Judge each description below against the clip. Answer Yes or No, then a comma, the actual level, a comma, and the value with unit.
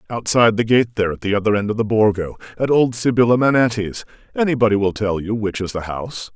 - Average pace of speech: No, fast, 215 wpm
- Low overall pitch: Yes, low, 110 Hz